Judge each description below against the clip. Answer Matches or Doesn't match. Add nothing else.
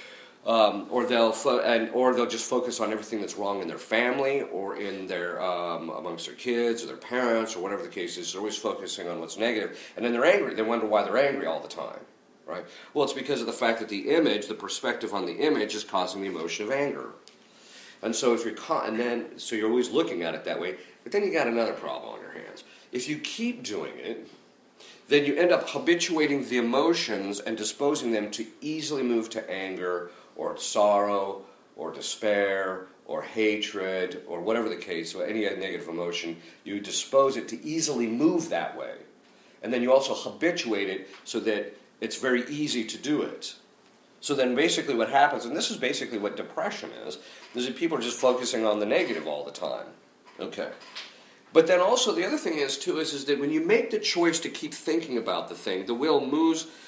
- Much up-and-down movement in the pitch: Matches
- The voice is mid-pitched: Doesn't match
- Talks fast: Matches